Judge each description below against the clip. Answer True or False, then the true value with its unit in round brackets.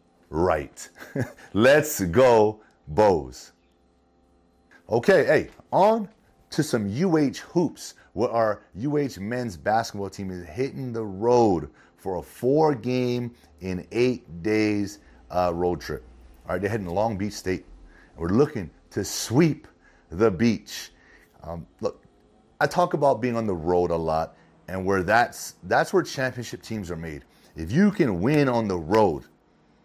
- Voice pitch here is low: True (105 Hz)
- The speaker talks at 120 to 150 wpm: True (145 wpm)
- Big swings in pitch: True (6.1 semitones)